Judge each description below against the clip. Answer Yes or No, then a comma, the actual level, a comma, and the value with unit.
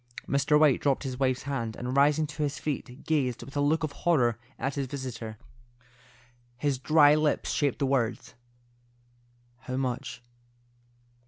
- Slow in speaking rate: No, average, 150 wpm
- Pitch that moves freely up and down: No, narrow, 2.6 semitones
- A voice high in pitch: No, medium, 140 Hz